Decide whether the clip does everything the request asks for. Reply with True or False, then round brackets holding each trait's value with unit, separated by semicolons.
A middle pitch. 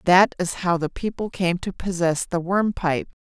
True (180 Hz)